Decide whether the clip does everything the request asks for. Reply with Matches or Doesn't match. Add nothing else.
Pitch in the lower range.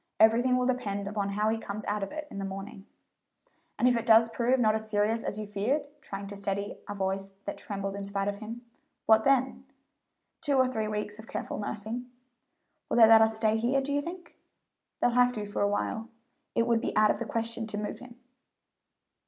Doesn't match